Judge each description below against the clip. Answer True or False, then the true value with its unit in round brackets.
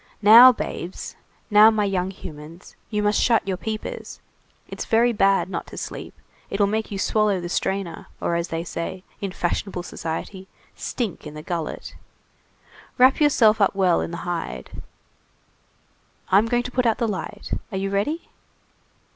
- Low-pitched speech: False (195 Hz)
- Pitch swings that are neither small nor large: True (3.7 semitones)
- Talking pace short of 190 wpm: True (160 wpm)